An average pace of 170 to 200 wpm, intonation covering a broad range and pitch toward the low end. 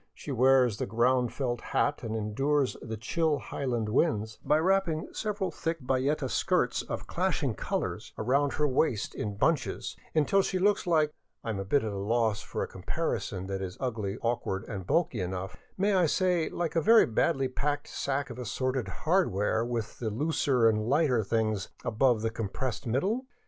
Yes: average, 180 wpm; wide, 5.7 semitones; low, 130 Hz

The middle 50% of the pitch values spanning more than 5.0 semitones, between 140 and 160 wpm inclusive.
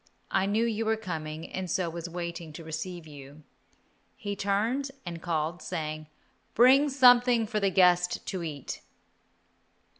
Yes: wide, 5.4 semitones; average, 145 wpm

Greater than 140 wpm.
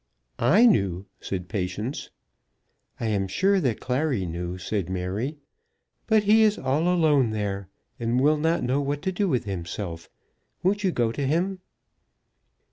Yes: average, 150 wpm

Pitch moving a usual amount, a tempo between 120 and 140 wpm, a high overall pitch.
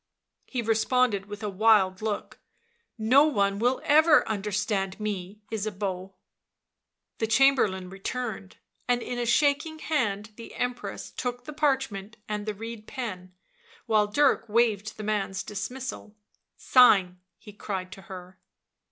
Yes: average, 3.9 semitones; slow, 135 wpm; high, 215 Hz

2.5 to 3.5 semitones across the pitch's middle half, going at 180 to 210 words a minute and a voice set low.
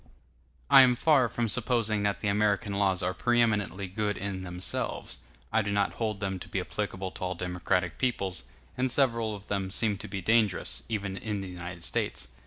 Yes: average, 3.1 semitones; average, 190 wpm; low, 100 Hz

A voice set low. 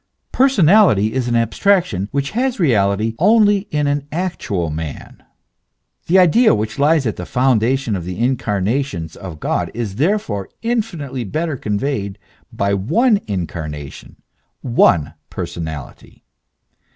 Yes: low, 125 Hz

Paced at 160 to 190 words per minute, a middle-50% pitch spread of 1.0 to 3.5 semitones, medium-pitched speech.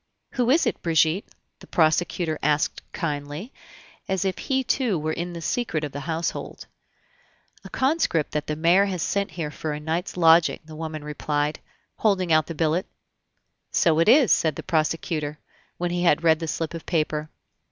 Yes: average, 175 wpm; average, 2.9 semitones; medium, 165 Hz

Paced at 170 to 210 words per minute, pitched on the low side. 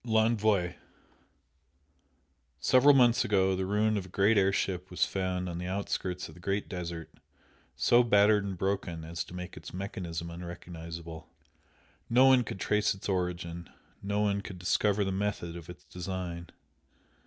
No: average, 155 wpm; very low, 95 Hz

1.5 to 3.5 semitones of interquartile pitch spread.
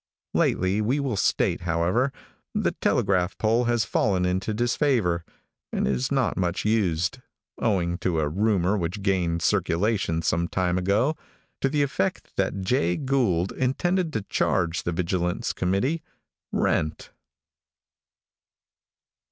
No: average, 5.2 semitones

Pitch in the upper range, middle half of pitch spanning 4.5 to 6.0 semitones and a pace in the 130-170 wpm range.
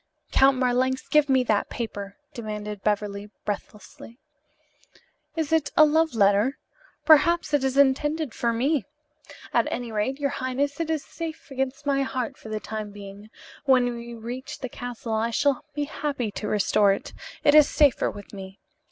Yes: very high, 255 Hz; average, 5.1 semitones; average, 165 wpm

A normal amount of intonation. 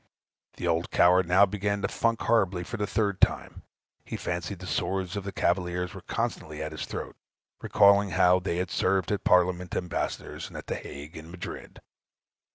No: narrow, 2.3 semitones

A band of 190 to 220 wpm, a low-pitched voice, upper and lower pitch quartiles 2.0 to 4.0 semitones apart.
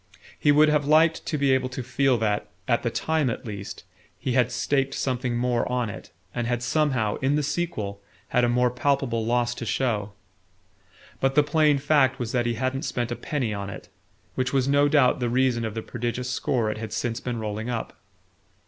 Yes: fast, 205 wpm; low, 125 Hz; average, 2.9 semitones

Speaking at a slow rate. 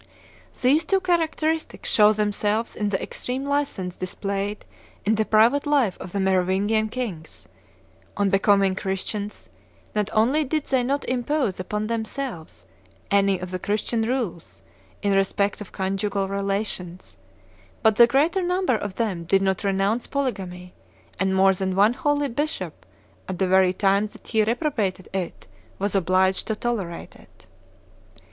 No: average, 145 wpm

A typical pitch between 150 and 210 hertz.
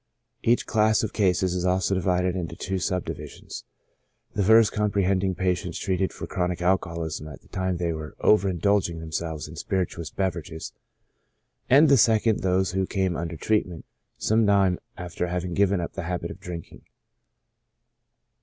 No: very low, 90 Hz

